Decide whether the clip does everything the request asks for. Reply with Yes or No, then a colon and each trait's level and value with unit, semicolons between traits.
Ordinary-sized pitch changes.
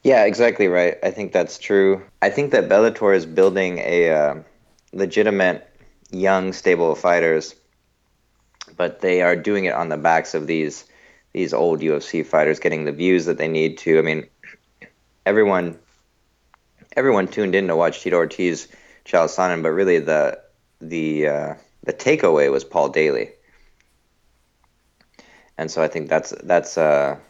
Yes: average, 3.7 semitones